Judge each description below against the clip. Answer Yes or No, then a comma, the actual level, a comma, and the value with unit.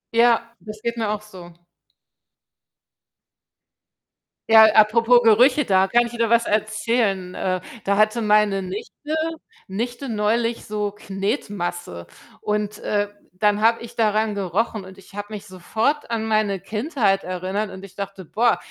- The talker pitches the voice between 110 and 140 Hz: No, high, 210 Hz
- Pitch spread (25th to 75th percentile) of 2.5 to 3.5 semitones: Yes, average, 2.8 semitones